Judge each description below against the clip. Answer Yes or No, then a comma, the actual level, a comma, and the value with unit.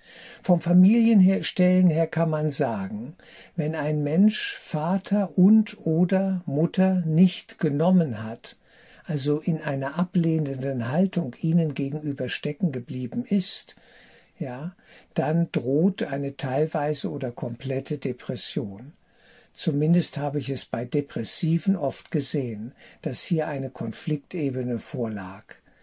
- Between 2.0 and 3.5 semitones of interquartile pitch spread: No, average, 4.8 semitones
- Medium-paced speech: No, slow, 110 wpm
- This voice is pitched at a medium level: Yes, medium, 155 Hz